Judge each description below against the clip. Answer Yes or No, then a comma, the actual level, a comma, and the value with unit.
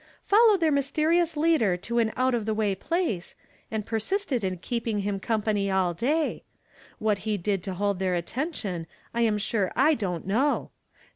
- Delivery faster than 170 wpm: Yes, average, 180 wpm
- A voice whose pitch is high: Yes, high, 220 Hz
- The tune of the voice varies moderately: No, wide, 6.4 semitones